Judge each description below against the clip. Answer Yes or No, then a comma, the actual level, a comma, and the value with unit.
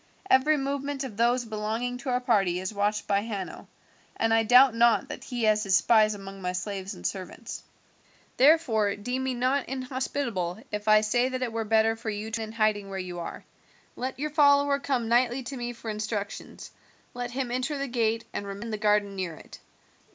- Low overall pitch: No, high, 225 Hz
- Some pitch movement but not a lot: Yes, average, 3.7 semitones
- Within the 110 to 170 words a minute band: No, fast, 205 wpm